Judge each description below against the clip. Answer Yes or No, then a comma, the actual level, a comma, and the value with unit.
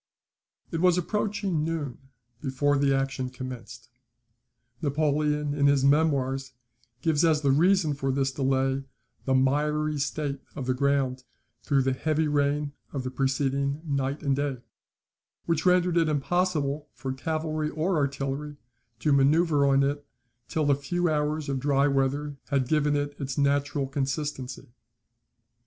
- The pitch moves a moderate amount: No, narrow, 2.1 semitones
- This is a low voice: No, medium, 145 Hz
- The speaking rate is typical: Yes, average, 145 wpm